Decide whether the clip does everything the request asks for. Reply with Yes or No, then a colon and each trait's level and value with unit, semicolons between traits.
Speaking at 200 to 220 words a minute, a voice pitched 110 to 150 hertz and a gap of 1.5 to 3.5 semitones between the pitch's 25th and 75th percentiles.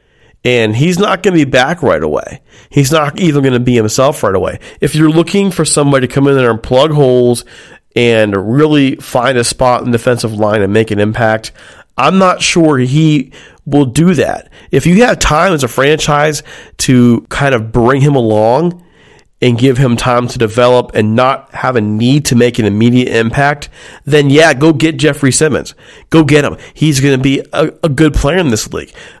No: fast, 205 wpm; low, 135 Hz; average, 4.1 semitones